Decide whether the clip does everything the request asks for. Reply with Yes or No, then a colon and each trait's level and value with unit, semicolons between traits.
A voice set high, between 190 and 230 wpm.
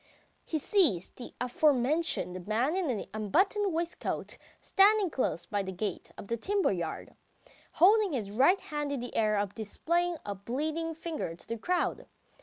No: very high, 275 Hz; average, 160 wpm